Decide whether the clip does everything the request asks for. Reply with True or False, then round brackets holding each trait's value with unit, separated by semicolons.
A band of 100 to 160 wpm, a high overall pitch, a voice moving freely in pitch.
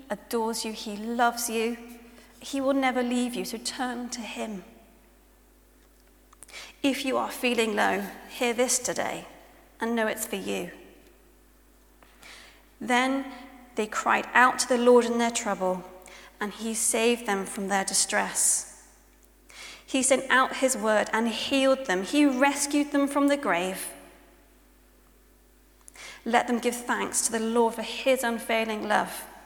False (140 wpm; 235 Hz; 2.6 semitones)